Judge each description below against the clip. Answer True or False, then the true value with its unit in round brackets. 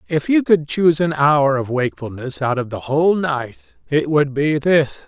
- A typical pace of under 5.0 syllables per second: True (4.6 syllables/s)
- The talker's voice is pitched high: False (145 Hz)